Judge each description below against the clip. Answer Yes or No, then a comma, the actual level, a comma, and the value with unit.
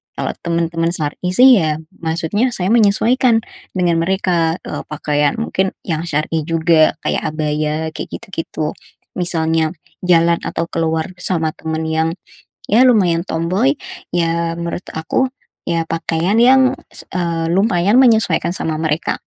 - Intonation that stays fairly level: No, average, 3.0 semitones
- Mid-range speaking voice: Yes, medium, 170 Hz